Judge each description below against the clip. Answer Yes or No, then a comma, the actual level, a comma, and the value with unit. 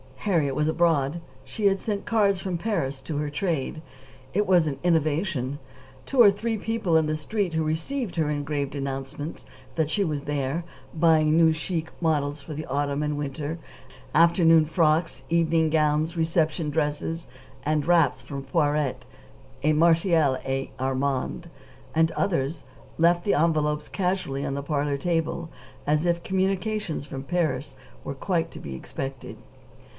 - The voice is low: No, medium, 155 Hz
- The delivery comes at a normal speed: Yes, average, 150 wpm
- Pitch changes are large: No, average, 3.0 semitones